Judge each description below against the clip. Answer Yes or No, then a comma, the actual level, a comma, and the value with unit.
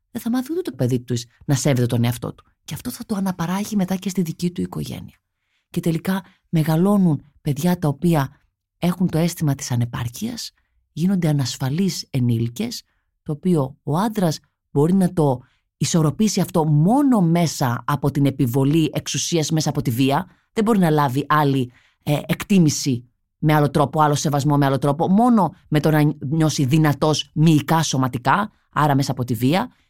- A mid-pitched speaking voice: Yes, medium, 150 Hz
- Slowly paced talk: No, fast, 170 wpm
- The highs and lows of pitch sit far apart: No, average, 4.4 semitones